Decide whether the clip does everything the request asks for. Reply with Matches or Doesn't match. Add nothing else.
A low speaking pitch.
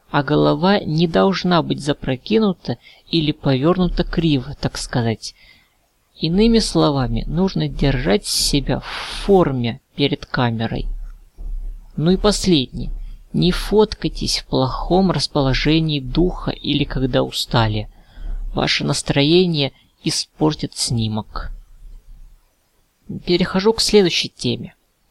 Doesn't match